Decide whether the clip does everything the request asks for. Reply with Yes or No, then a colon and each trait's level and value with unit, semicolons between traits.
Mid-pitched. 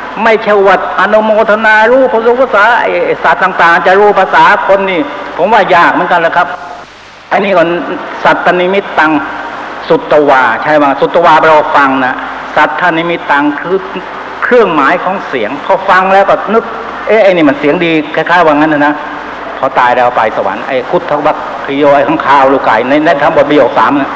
Yes: medium, 175 Hz